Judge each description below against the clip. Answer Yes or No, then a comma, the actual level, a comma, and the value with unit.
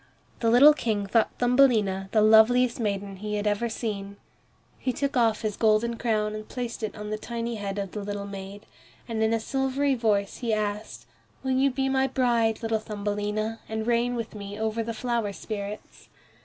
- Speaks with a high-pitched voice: Yes, high, 220 Hz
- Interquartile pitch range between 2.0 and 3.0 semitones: Yes, narrow, 2.5 semitones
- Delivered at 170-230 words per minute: Yes, average, 185 wpm